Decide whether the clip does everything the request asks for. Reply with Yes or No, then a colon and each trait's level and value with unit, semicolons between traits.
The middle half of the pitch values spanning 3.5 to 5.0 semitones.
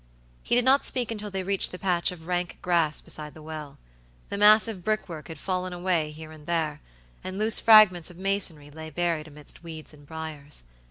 Yes: average, 3.8 semitones